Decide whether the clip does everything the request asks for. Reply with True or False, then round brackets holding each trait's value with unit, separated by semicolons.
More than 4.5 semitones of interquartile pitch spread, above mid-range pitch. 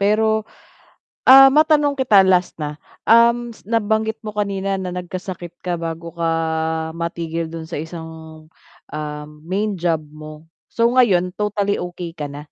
False (5.0 semitones; 180 Hz)